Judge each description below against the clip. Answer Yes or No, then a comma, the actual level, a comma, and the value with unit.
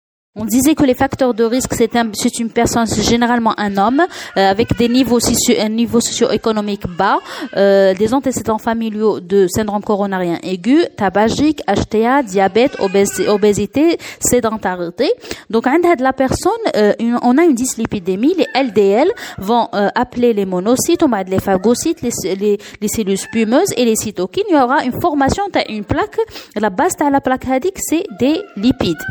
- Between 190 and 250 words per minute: No, average, 175 wpm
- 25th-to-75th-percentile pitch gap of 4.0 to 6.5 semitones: Yes, average, 4.6 semitones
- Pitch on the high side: Yes, high, 235 Hz